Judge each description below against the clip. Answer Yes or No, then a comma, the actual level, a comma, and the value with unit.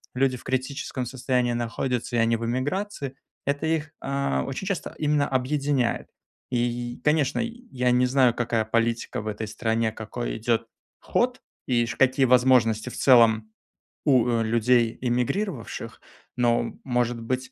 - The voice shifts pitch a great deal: No, average, 2.8 semitones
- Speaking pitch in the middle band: No, low, 125 Hz